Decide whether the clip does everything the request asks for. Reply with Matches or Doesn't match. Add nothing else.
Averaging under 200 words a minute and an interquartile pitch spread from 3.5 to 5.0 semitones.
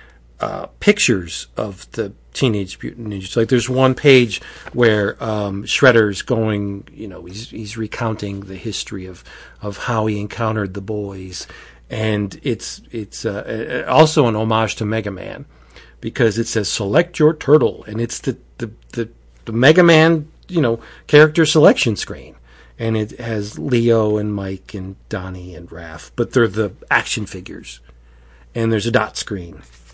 Doesn't match